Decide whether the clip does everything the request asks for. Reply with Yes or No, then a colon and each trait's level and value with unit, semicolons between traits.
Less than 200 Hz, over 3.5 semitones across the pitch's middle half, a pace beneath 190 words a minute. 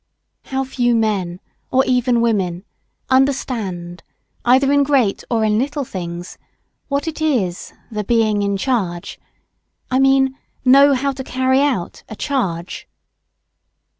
No: high, 245 Hz; average, 5.3 semitones; slow, 135 wpm